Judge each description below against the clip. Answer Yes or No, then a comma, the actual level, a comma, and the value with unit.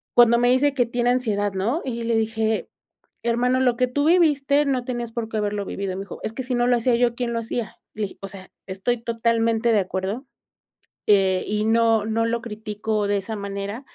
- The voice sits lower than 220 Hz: No, high, 230 Hz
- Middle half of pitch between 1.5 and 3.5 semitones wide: Yes, average, 2.7 semitones